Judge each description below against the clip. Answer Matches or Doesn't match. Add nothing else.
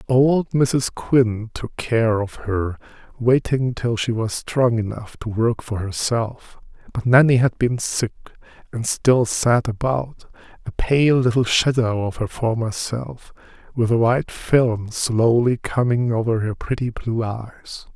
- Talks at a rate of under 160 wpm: Matches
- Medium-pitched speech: Doesn't match